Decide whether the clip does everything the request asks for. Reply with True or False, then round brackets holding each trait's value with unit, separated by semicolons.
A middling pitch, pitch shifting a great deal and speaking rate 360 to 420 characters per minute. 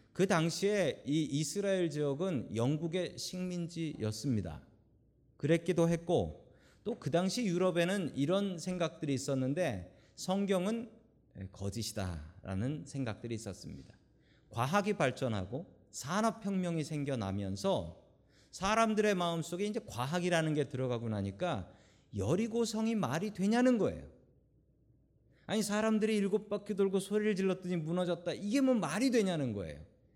False (170 Hz; 7.8 semitones; 300 characters per minute)